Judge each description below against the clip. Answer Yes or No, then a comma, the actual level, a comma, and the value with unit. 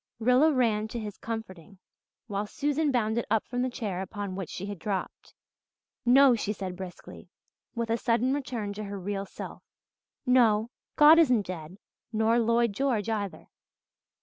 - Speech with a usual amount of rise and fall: Yes, average, 3.5 semitones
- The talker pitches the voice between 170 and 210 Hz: No, high, 220 Hz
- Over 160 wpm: No, average, 155 wpm